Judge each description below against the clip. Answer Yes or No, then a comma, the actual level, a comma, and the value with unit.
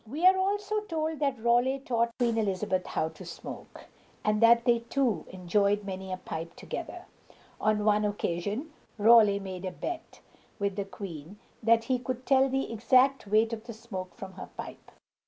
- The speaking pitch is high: Yes, high, 225 Hz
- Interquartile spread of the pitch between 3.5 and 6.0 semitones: Yes, average, 4.5 semitones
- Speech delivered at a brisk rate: No, average, 175 wpm